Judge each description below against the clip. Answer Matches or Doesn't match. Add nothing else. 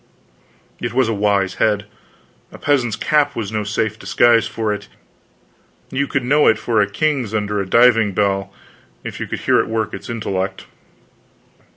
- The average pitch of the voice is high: Doesn't match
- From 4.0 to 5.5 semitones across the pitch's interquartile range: Doesn't match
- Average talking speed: Matches